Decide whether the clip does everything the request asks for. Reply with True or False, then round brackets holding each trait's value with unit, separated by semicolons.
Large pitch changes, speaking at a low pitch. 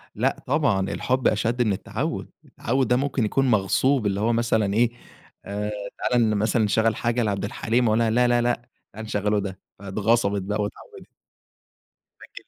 False (2.8 semitones; 110 Hz)